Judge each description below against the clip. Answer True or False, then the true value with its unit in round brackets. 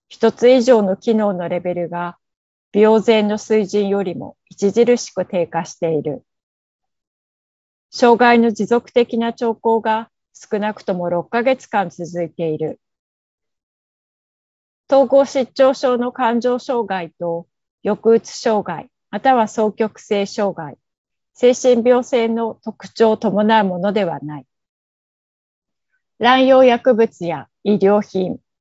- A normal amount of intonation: True (4.6 semitones)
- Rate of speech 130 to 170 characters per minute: False (210 characters per minute)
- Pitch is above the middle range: True (215 Hz)